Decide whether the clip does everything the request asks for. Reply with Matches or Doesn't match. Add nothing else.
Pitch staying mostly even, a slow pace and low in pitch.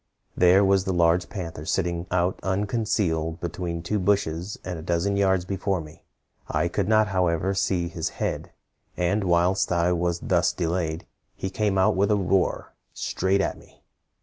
Doesn't match